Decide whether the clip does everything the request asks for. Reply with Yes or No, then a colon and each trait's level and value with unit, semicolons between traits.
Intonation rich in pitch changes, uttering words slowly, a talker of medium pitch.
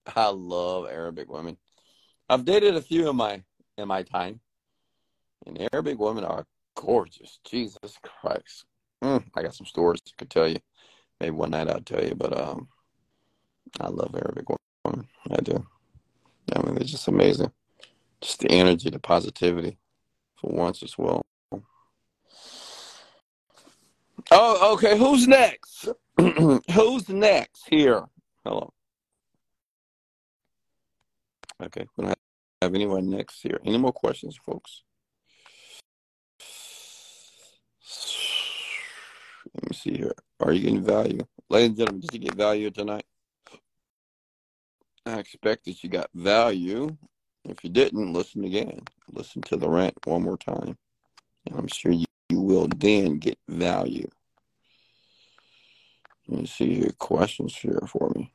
No: wide, 8.9 semitones; slow, 130 wpm; low, 100 Hz